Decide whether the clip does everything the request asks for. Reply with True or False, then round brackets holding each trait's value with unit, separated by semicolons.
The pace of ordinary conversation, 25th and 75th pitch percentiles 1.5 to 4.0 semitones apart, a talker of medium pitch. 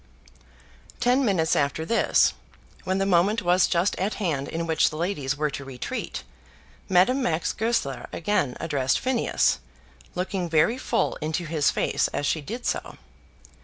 False (150 wpm; 5.1 semitones; 170 Hz)